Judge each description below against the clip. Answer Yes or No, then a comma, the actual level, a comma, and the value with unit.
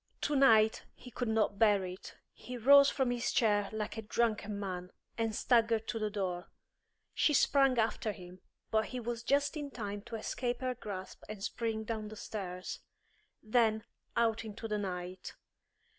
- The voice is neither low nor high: No, high, 220 Hz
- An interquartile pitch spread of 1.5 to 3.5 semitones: Yes, average, 2.8 semitones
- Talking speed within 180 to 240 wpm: No, average, 165 wpm